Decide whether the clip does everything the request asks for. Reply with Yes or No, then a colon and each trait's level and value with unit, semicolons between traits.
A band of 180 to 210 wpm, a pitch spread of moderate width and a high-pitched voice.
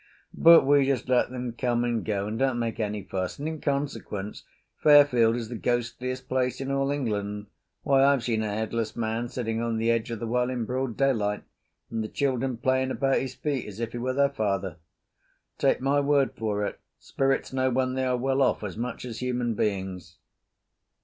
No: average, 200 wpm; average, 3.2 semitones; low, 120 Hz